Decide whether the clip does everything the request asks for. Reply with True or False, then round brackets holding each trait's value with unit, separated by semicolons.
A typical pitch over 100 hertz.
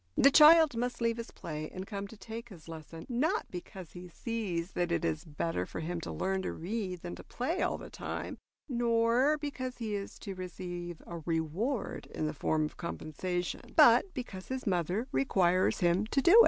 True (190 Hz)